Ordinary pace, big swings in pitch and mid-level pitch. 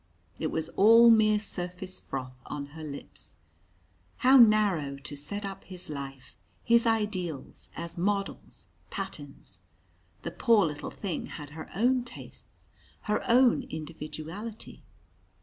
No: slow, 125 wpm; wide, 6.3 semitones; medium, 180 Hz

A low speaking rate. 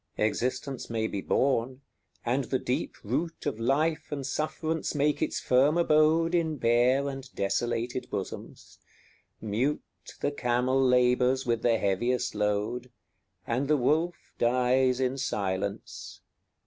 Yes: slow, 130 wpm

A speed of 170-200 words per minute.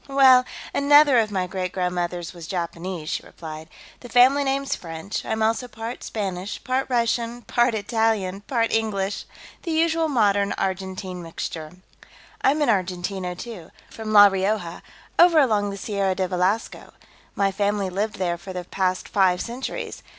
No: average, 150 wpm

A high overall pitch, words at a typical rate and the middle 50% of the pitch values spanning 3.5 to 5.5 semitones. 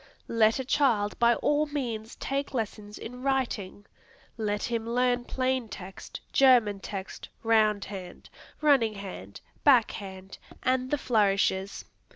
No: high, 225 Hz; slow, 130 wpm; average, 4.1 semitones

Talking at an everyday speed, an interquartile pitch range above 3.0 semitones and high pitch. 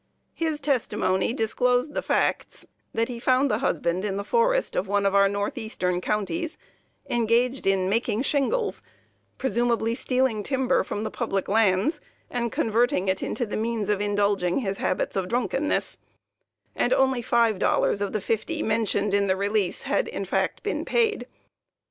Yes: average, 160 wpm; average, 4.4 semitones; high, 225 Hz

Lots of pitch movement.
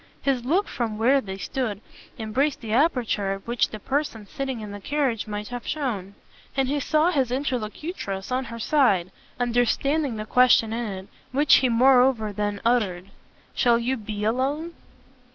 No: average, 4.1 semitones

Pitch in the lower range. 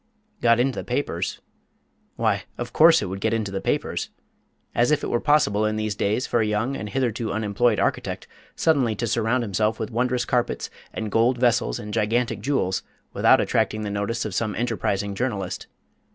Yes: low, 115 Hz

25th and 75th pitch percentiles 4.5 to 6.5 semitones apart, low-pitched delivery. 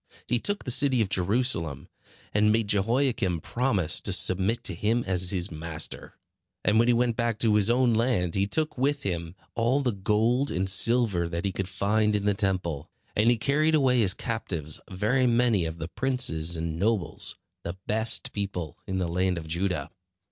Yes: average, 5.0 semitones; low, 105 Hz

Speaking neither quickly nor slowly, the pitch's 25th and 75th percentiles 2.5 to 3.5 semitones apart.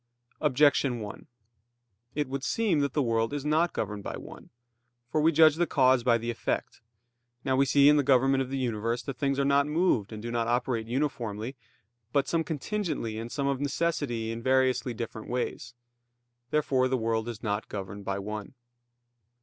No: average, 180 wpm; average, 3.9 semitones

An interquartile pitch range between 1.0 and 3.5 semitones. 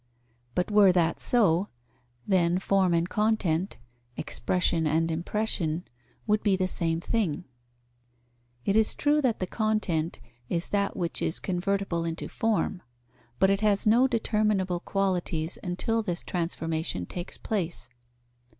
No: average, 3.9 semitones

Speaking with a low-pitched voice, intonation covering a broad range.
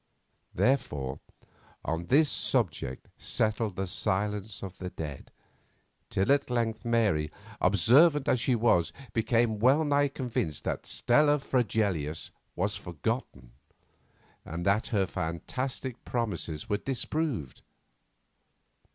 Yes: low, 110 Hz; wide, 6.4 semitones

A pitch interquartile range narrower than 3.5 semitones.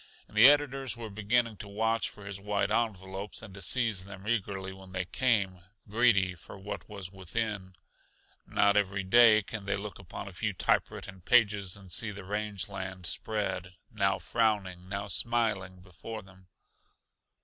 Yes: narrow, 2.4 semitones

